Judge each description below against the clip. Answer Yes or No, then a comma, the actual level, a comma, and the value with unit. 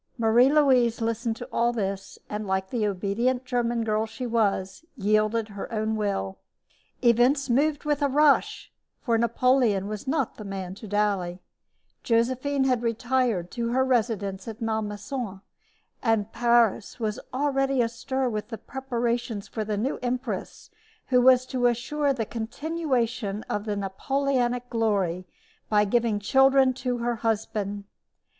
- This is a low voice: No, high, 235 Hz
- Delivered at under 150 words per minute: Yes, average, 140 wpm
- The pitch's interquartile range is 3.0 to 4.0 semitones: Yes, average, 3.3 semitones